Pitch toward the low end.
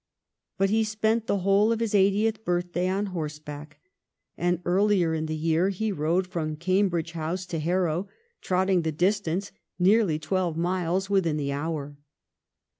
No: medium, 180 Hz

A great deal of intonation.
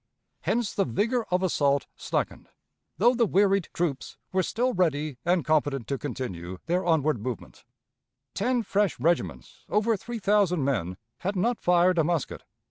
Yes: wide, 6.4 semitones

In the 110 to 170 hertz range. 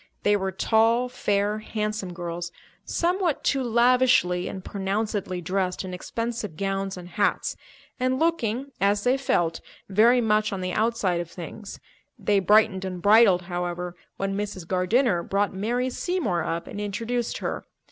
No: high, 205 Hz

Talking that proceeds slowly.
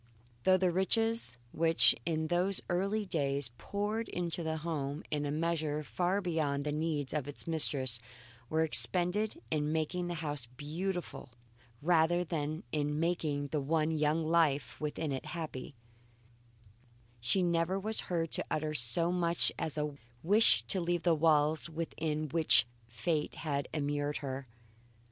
No: average, 145 wpm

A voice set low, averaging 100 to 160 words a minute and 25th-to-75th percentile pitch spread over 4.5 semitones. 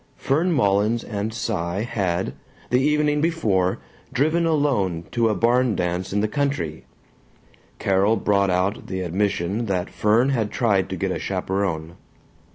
Yes: low, 105 Hz; average, 145 wpm; average, 5.0 semitones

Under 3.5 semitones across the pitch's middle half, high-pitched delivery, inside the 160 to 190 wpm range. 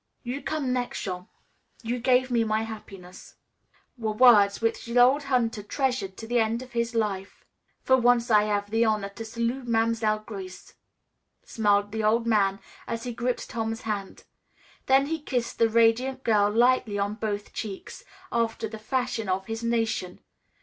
Yes: average, 2.7 semitones; high, 225 Hz; average, 165 wpm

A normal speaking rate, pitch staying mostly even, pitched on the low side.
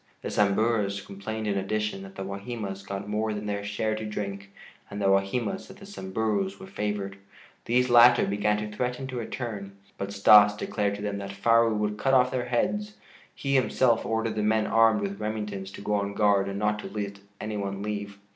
Yes: average, 195 wpm; narrow, 2.3 semitones; low, 105 Hz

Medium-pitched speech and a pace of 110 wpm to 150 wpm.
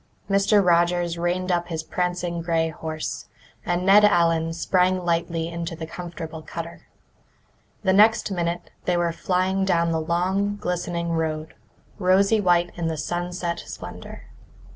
Yes: medium, 175 Hz; average, 140 wpm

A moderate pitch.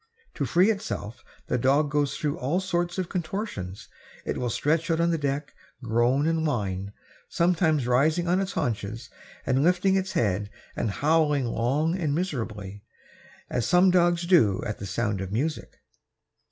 Yes: medium, 150 Hz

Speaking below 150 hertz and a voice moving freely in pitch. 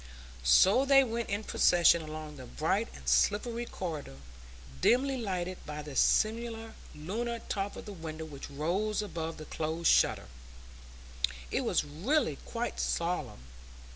No: medium, 175 Hz; wide, 6.5 semitones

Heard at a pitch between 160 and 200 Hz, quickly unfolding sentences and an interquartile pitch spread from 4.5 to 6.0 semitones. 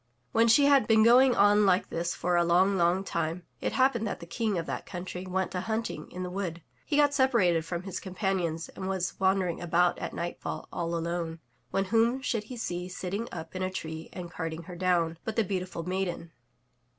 No: medium, 185 Hz; fast, 215 wpm; average, 3.5 semitones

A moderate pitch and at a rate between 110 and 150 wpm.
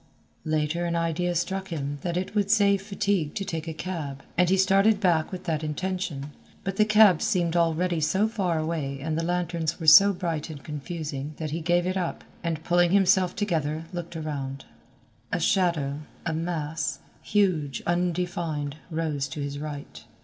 No: medium, 170 Hz; average, 170 wpm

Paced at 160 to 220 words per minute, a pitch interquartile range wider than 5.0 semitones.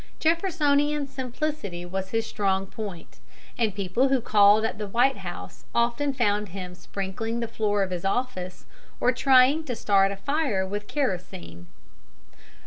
No: average, 145 wpm; wide, 5.4 semitones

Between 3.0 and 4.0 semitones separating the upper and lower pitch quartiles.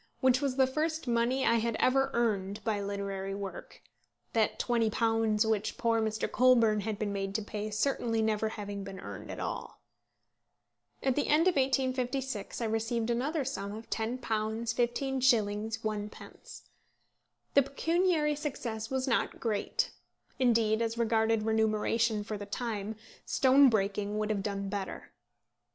Yes: average, 3.3 semitones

